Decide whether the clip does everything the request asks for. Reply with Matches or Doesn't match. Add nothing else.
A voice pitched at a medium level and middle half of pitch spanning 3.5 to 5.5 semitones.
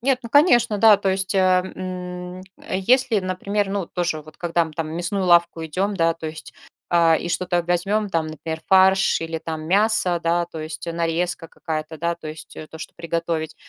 Doesn't match